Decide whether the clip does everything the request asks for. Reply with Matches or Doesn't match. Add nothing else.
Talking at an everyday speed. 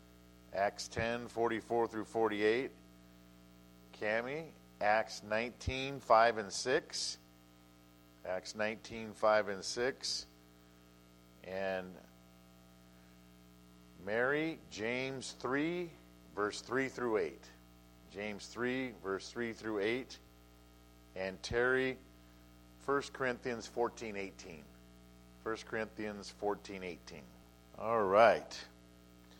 Doesn't match